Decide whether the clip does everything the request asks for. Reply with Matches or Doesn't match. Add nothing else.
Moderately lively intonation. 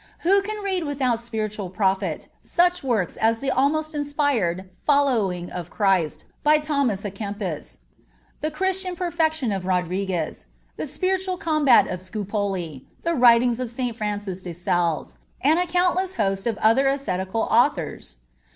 Doesn't match